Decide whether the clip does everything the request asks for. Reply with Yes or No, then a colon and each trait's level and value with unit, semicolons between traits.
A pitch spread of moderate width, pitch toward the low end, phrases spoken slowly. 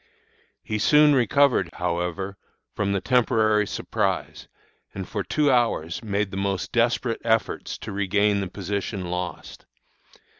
Yes: average, 3.3 semitones; low, 100 Hz; slow, 120 wpm